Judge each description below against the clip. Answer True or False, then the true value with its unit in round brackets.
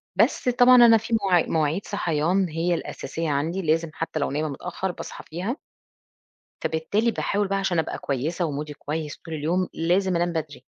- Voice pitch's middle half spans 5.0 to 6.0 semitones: False (3.7 semitones)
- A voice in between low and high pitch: True (170 Hz)